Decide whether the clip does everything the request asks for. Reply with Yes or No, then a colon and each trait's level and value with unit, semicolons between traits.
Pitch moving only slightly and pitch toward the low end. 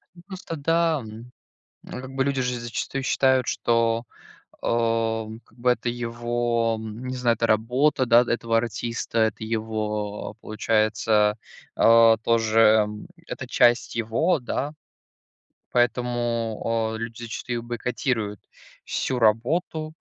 Yes: narrow, 1.9 semitones; low, 115 Hz